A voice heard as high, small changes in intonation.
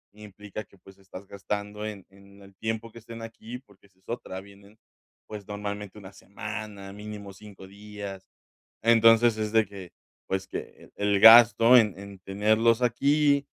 No: low, 105 Hz; narrow, 2.3 semitones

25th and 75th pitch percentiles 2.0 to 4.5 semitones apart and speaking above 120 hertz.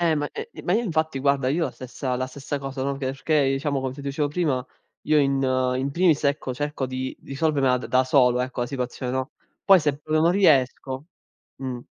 Yes: average, 2.7 semitones; medium, 140 Hz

